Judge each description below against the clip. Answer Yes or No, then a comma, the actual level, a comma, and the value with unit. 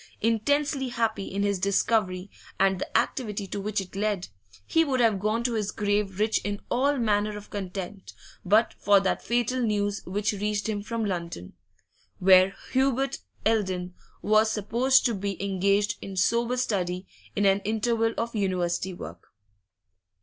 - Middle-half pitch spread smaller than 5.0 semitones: Yes, average, 2.8 semitones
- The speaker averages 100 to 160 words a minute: Yes, average, 155 wpm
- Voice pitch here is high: Yes, high, 205 Hz